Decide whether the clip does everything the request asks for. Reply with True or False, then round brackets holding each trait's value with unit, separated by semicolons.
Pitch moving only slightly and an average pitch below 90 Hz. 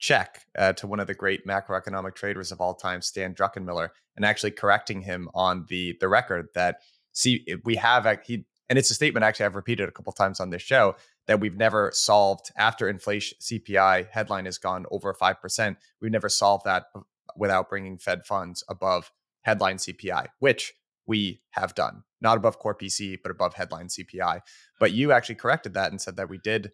False (2.3 semitones; 100 Hz)